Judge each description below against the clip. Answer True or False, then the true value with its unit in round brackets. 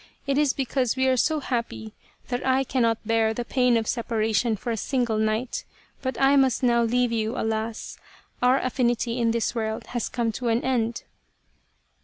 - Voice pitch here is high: True (240 Hz)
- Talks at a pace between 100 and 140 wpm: False (185 wpm)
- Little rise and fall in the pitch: True (2.3 semitones)